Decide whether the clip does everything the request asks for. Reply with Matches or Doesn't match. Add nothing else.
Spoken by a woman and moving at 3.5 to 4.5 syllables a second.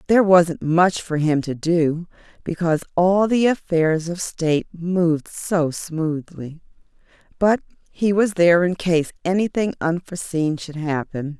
Matches